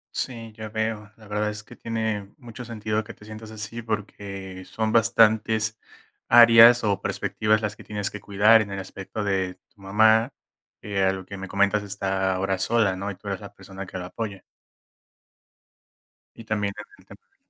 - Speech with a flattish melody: Yes, narrow, 2.1 semitones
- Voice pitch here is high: No, low, 105 Hz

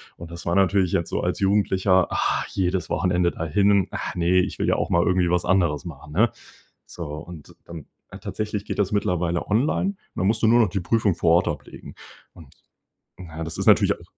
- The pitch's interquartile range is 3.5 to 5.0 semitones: No, average, 2.7 semitones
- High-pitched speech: No, very low, 90 Hz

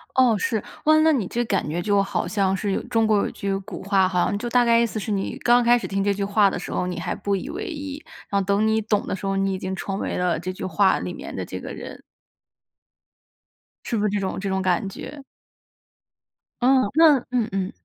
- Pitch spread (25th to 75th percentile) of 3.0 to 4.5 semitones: Yes, average, 3.4 semitones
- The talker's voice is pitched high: Yes, high, 200 Hz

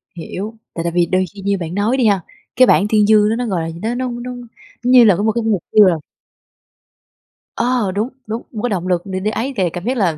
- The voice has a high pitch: Yes, high, 210 Hz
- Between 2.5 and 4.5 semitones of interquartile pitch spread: Yes, average, 3.9 semitones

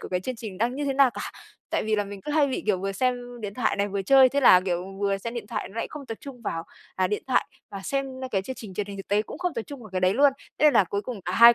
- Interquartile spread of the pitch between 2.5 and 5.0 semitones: Yes, average, 4.7 semitones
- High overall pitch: Yes, high, 220 Hz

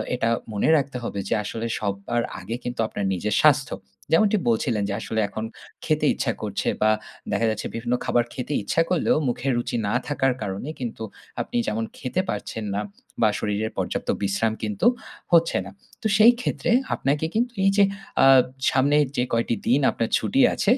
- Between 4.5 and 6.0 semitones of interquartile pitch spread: Yes, average, 4.9 semitones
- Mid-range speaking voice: No, low, 120 Hz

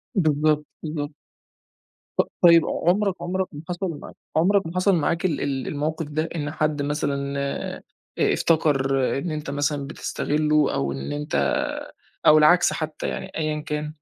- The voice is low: No, medium, 150 Hz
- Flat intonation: Yes, narrow, 2.3 semitones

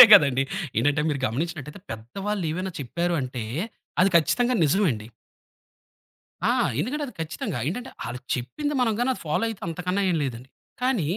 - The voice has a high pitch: No, medium, 170 Hz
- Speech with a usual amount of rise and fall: No, wide, 7.3 semitones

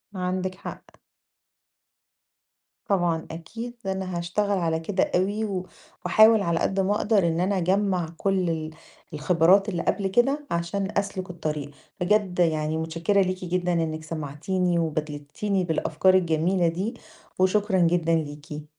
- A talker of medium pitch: Yes, medium, 180 Hz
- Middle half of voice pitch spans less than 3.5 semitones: Yes, average, 3.1 semitones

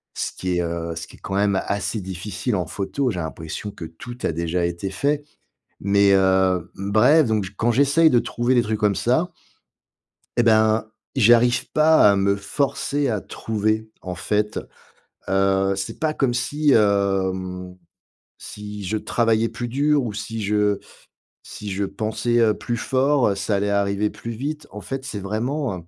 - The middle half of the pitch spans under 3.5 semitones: No, average, 3.8 semitones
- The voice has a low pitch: Yes, low, 105 Hz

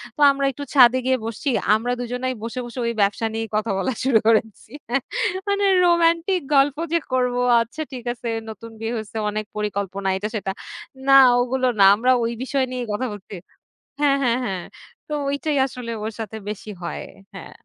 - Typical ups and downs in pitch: Yes, average, 3.6 semitones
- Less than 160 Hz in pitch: No, high, 240 Hz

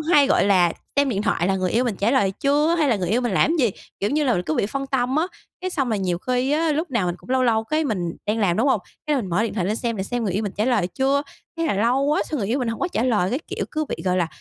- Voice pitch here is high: Yes, high, 235 Hz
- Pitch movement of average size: No, wide, 5.9 semitones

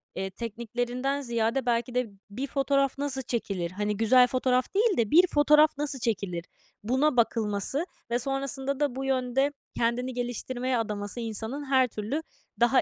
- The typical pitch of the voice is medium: No, very high, 250 Hz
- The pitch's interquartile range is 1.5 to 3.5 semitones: Yes, average, 3.2 semitones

